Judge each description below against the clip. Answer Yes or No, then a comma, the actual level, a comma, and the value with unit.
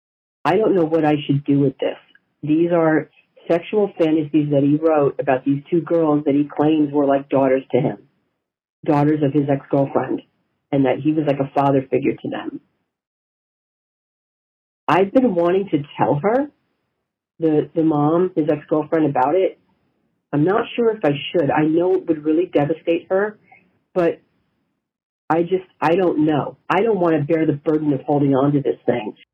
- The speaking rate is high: No, average, 180 wpm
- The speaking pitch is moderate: Yes, medium, 155 Hz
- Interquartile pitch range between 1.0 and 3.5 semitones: Yes, average, 2.9 semitones